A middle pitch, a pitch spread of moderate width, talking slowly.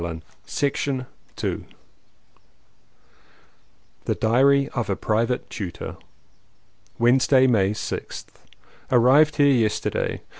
No: low, 125 Hz; average, 4.1 semitones; slow, 80 wpm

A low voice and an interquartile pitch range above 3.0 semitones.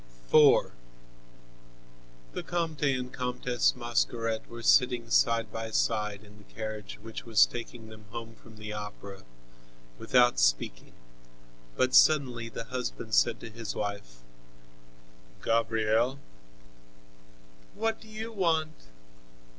No: low, 115 Hz; average, 2.7 semitones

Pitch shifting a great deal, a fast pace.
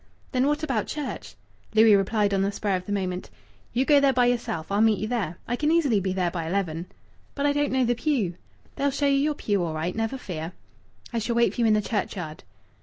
Yes: wide, 5.9 semitones; fast, 240 wpm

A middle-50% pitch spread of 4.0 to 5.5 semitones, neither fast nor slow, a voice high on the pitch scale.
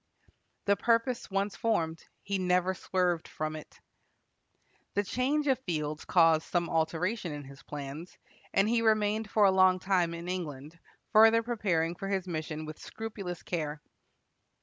No: average, 4.6 semitones; average, 145 wpm; medium, 180 Hz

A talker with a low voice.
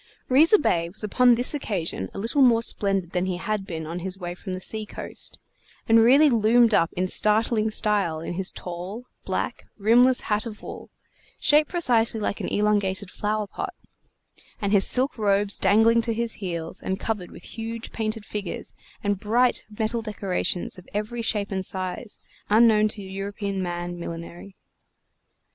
No: high, 210 Hz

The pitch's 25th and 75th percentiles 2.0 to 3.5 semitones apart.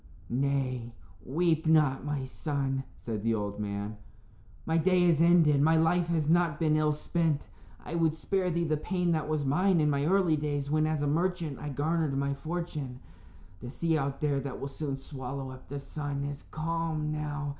Yes: average, 3.0 semitones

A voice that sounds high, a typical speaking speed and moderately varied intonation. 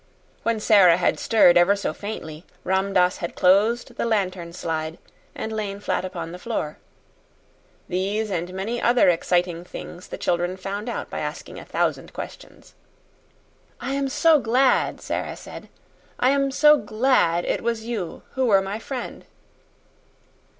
Yes: high, 200 Hz; average, 150 wpm; average, 4.7 semitones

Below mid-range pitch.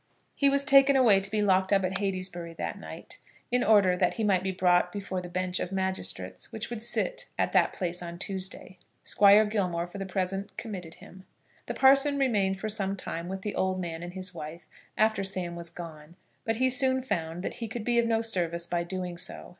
No: high, 190 Hz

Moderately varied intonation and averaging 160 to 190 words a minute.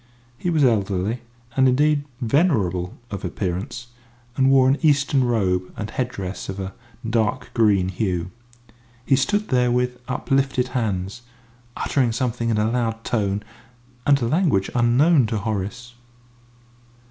No: average, 4.7 semitones; slow, 135 wpm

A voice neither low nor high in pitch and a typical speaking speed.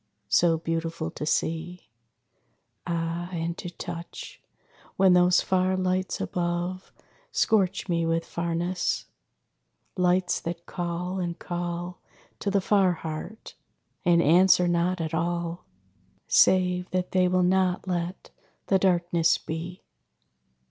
No: medium, 175 Hz; slow, 115 wpm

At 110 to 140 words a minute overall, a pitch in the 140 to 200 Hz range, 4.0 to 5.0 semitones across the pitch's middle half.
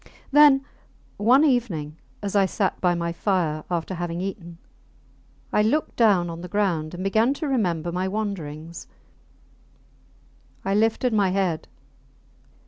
Yes: slow, 135 wpm; high, 190 Hz; average, 4.4 semitones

